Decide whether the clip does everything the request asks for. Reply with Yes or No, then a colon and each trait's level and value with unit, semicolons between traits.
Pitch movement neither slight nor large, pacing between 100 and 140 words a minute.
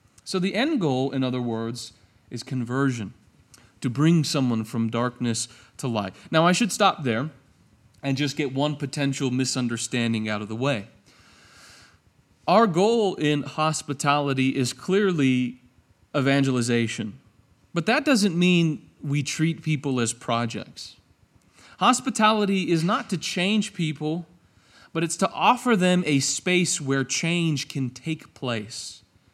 No: wide, 6.1 semitones; slow, 135 wpm